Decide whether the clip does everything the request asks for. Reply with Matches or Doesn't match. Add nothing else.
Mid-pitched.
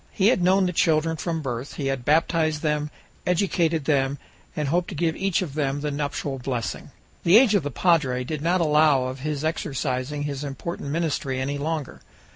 Matches